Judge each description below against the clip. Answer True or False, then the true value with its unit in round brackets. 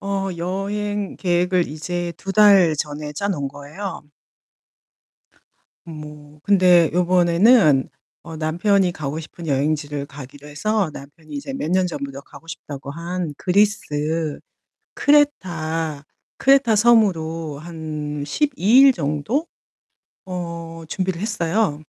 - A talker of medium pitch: True (170 Hz)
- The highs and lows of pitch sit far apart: False (4.7 semitones)